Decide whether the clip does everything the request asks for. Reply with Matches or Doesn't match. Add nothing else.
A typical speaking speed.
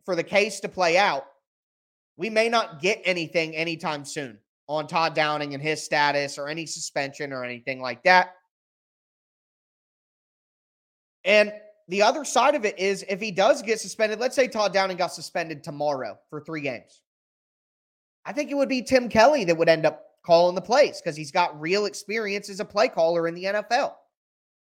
Matches